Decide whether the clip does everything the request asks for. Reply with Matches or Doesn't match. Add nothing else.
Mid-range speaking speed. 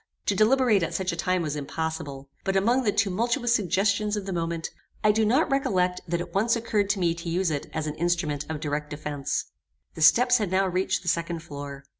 Doesn't match